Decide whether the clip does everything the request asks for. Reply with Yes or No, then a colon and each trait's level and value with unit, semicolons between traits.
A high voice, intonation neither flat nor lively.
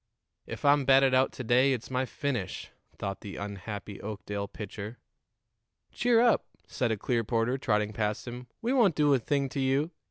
No: low, 125 Hz; average, 4.7 semitones